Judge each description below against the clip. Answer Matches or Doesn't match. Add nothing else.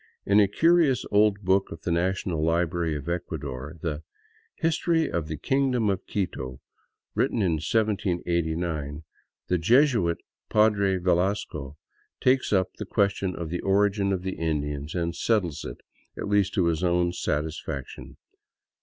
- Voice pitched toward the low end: Matches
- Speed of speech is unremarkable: Matches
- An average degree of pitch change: Matches